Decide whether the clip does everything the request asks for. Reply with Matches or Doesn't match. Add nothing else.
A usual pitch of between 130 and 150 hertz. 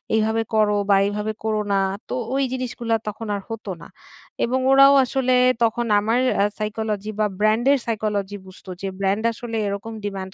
Doesn't match